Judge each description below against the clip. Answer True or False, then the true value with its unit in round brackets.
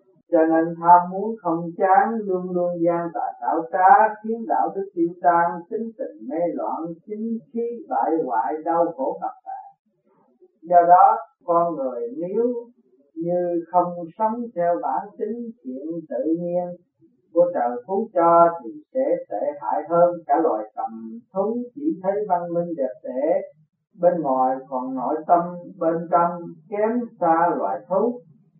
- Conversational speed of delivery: False (155 wpm)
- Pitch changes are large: False (4.7 semitones)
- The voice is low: False (175 Hz)